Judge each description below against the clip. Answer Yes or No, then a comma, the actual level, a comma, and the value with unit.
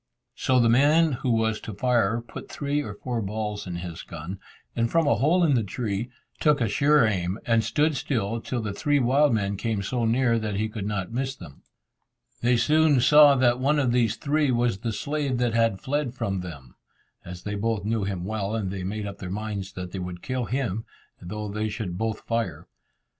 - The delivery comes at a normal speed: No, fast, 210 wpm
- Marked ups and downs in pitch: No, average, 4.3 semitones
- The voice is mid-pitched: No, low, 115 Hz